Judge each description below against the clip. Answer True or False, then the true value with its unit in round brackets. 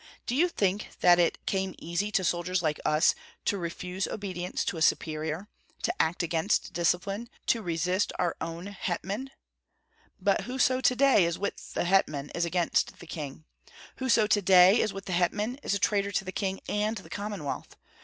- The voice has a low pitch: False (185 Hz)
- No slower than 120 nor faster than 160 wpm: False (180 wpm)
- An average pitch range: True (3.2 semitones)